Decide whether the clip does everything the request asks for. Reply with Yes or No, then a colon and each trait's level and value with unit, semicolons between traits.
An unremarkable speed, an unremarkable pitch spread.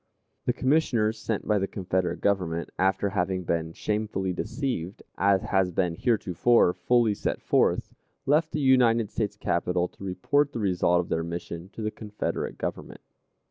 Yes: average, 155 wpm; average, 4.3 semitones